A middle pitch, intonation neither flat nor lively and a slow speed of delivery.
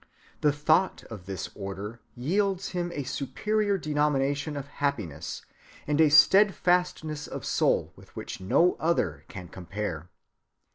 No: medium, 145 Hz; wide, 8.8 semitones; slow, 130 wpm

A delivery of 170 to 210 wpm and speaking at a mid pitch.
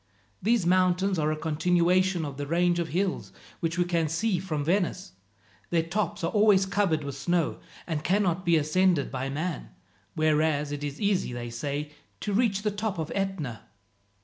Yes: average, 175 wpm; medium, 170 Hz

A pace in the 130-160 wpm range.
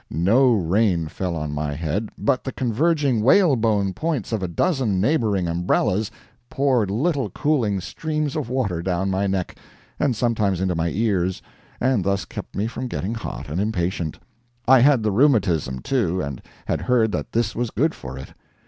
No: average, 170 wpm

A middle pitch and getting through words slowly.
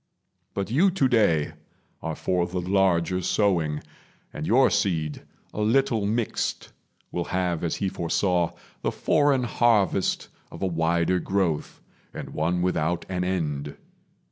No: very low, 90 Hz; slow, 130 wpm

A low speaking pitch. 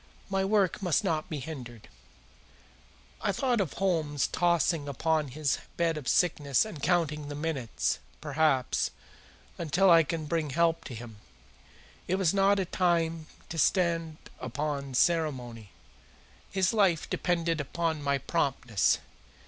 No: medium, 160 Hz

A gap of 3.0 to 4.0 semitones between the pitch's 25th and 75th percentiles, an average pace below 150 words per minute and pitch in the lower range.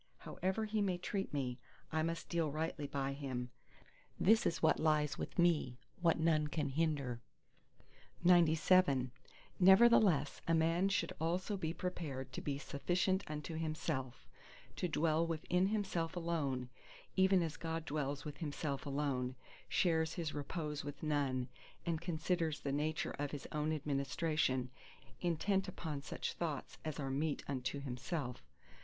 No: average, 3.4 semitones; average, 140 wpm; medium, 155 Hz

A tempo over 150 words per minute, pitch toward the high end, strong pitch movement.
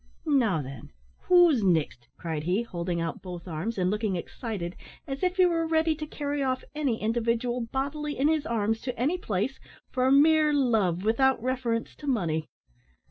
Yes: average, 170 wpm; high, 235 Hz; wide, 7.7 semitones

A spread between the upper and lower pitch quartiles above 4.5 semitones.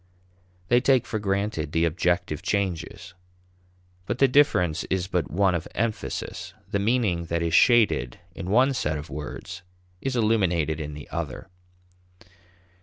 Yes: average, 5.2 semitones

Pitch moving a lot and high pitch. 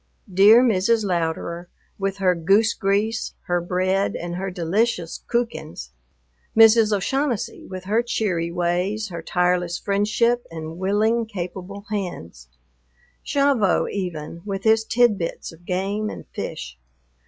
No: average, 3.8 semitones; high, 195 Hz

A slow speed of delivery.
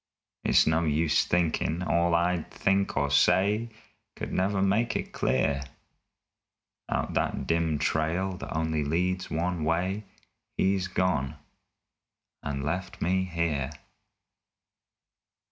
Yes: slow, 110 wpm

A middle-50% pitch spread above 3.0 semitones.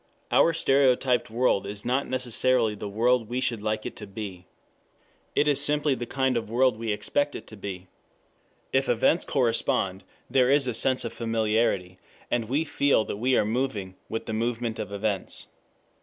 Yes: average, 3.4 semitones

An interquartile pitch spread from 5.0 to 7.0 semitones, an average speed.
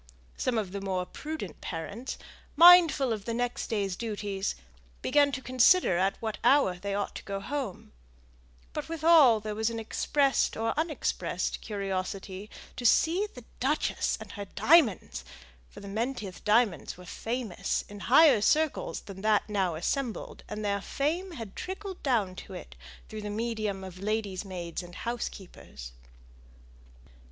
Yes: wide, 5.5 semitones; average, 150 wpm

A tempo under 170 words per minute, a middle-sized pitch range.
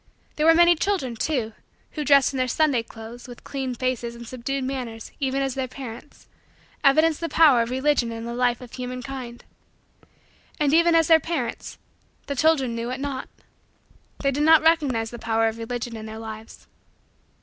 No: average, 180 wpm; average, 3.8 semitones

